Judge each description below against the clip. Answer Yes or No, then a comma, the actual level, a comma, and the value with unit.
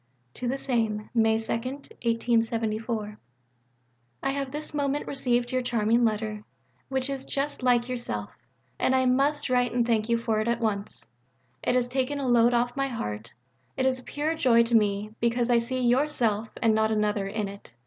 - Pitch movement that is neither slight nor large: Yes, average, 3.1 semitones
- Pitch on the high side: Yes, high, 235 Hz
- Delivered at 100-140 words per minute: No, average, 180 wpm